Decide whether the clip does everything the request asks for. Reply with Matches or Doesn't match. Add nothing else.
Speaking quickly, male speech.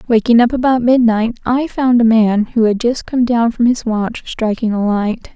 Doesn't match